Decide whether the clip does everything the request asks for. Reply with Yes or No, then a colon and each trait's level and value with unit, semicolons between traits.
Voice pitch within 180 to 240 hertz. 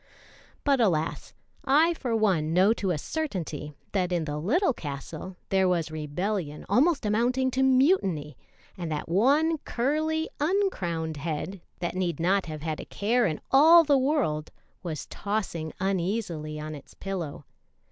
Yes: high, 190 Hz